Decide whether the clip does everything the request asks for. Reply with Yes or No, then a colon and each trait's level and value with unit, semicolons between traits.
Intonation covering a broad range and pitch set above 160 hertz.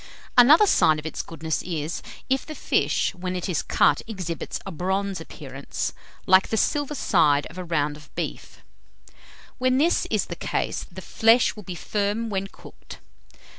Yes: wide, 5.9 semitones; medium, 185 Hz